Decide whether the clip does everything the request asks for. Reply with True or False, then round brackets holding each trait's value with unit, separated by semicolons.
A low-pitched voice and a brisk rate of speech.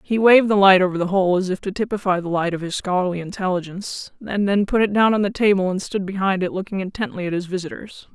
False (190 Hz; 250 wpm)